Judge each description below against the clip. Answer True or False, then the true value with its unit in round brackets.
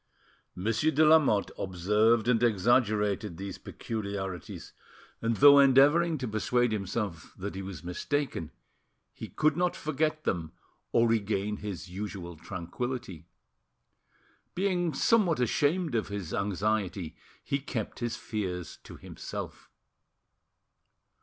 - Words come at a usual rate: False (115 wpm)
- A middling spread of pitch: False (6.1 semitones)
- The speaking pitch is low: True (110 Hz)